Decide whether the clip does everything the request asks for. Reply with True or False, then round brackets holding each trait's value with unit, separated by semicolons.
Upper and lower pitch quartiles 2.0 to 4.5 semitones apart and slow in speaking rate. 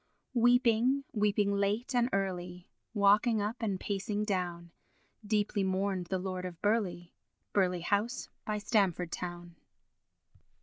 True (2.9 semitones; 120 wpm)